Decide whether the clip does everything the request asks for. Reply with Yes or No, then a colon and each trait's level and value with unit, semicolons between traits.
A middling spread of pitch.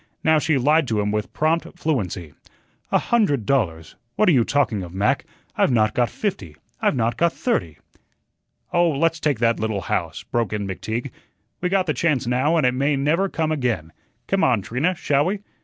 No: wide, 6.9 semitones